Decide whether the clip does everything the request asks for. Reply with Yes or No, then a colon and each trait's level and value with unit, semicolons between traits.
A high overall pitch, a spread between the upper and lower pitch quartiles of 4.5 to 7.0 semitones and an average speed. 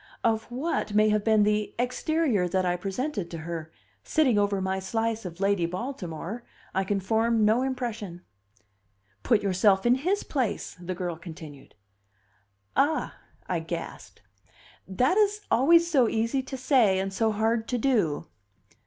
Yes: high, 215 Hz; average, 4.9 semitones; average, 150 wpm